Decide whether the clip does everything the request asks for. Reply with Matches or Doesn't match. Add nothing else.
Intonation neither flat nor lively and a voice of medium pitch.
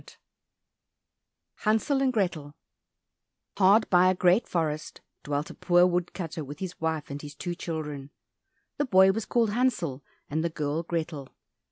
Matches